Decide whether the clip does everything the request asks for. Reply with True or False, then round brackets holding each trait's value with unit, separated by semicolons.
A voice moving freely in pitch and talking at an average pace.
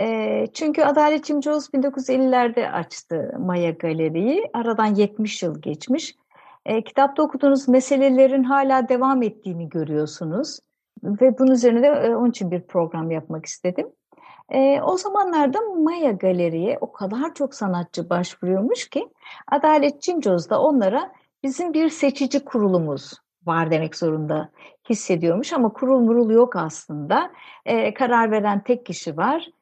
True (8.0 semitones; 120 wpm)